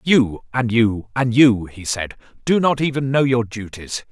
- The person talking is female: No, male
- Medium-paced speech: Yes, average, 190 wpm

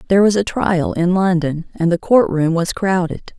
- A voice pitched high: No, medium, 180 Hz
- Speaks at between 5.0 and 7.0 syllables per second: No, 4.8 syllables/s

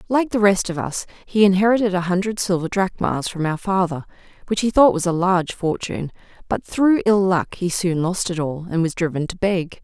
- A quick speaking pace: Yes, fast, 215 wpm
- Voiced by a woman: Yes, female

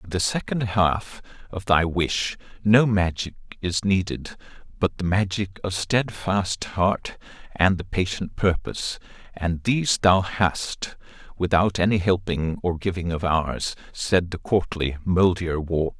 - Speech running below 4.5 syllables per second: Yes, 4.0 syllables/s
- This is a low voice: Yes, very low, 90 Hz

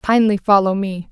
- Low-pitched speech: No, high, 200 Hz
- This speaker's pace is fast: No, average, 160 wpm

